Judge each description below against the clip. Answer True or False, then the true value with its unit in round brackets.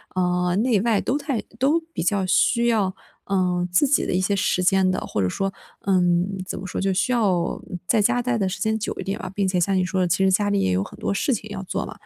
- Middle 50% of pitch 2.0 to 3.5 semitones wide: True (3.1 semitones)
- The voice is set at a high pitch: True (195 Hz)